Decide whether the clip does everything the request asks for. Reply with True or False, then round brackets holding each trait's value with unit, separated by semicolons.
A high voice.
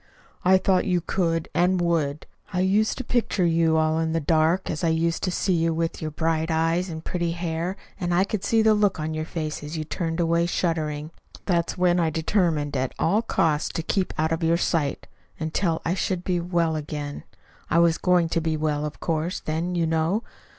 False (165 Hz)